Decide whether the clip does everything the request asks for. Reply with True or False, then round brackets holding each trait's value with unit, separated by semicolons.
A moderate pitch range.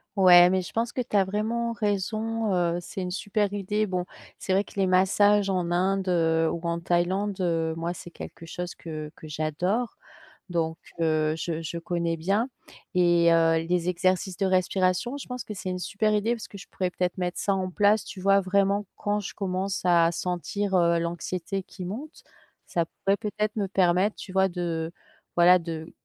True (3.0 semitones)